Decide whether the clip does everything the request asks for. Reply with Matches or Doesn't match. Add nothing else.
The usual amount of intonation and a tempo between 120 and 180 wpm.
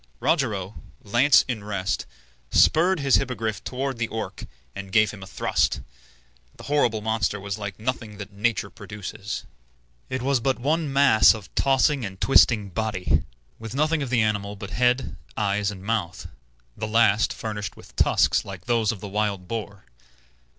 Matches